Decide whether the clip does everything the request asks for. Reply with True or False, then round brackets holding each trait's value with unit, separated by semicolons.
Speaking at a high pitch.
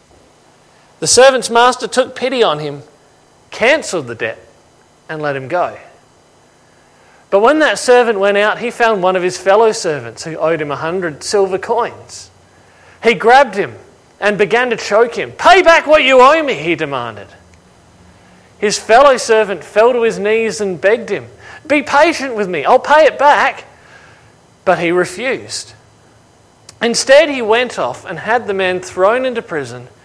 True (205 Hz)